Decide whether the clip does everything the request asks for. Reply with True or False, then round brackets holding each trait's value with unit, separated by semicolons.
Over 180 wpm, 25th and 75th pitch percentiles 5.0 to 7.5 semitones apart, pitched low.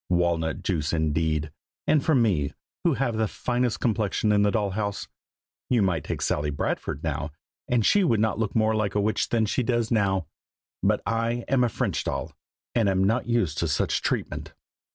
True (190 wpm; 5.5 semitones; 105 Hz)